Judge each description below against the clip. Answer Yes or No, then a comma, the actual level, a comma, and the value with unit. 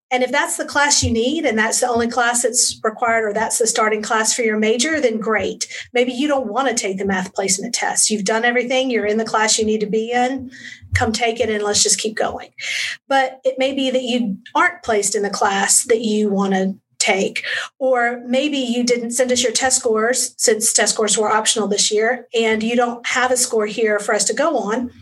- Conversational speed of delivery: No, fast, 235 wpm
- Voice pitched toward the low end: No, high, 235 Hz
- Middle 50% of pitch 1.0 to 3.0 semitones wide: Yes, narrow, 2.6 semitones